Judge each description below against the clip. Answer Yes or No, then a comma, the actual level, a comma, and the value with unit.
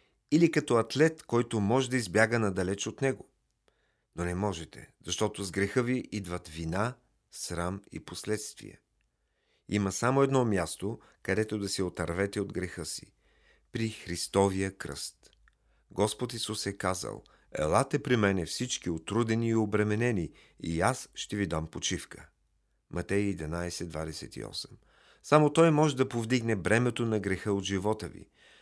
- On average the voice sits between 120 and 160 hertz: No, low, 105 Hz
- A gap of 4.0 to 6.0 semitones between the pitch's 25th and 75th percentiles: Yes, average, 4.6 semitones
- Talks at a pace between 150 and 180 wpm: No, average, 140 wpm